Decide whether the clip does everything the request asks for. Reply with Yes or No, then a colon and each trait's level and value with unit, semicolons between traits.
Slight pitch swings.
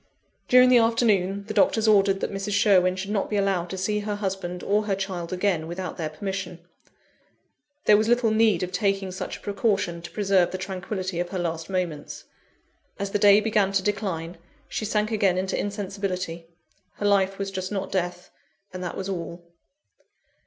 Yes: narrow, 2.2 semitones